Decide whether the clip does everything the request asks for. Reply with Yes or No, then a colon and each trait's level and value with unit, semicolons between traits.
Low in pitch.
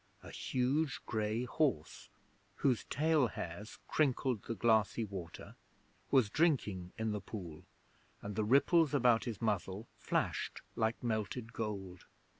Yes: low, 110 Hz